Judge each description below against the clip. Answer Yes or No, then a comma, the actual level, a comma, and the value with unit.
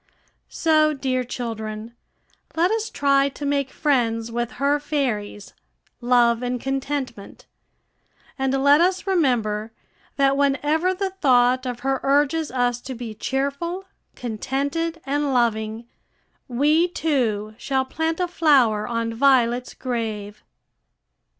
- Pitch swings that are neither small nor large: Yes, average, 3.7 semitones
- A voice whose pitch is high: Yes, very high, 265 Hz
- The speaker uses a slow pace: Yes, slow, 120 wpm